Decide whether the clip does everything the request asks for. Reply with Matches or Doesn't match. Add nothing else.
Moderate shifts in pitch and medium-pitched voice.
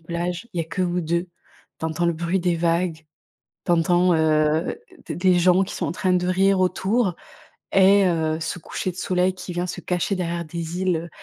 Doesn't match